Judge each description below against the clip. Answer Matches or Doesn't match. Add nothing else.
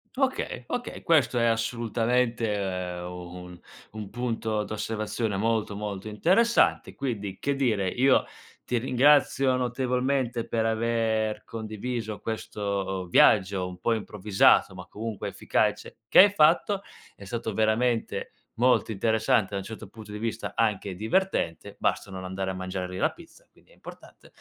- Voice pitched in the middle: Doesn't match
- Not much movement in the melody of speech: Doesn't match